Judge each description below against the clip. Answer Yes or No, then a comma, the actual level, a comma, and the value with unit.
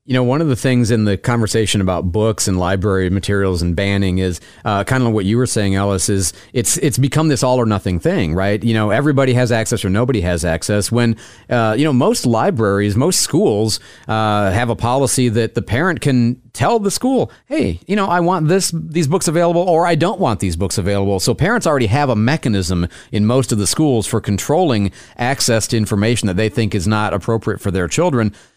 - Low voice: Yes, low, 115 Hz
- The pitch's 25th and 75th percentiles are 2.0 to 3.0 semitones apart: No, average, 4.6 semitones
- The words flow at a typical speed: No, fast, 220 wpm